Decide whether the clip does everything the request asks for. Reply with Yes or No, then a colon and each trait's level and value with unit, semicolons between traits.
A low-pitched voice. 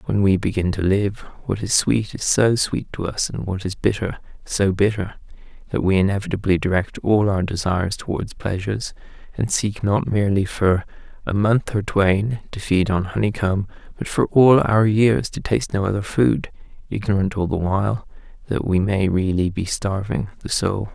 Yes: low, 100 Hz